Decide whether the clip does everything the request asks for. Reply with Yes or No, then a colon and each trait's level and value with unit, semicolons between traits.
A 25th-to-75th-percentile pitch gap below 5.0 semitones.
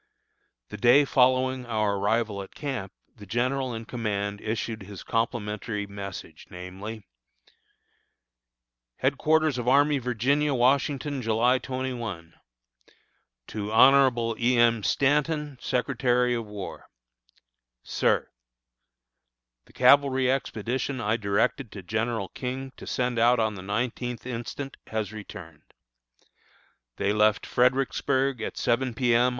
Yes: average, 3.5 semitones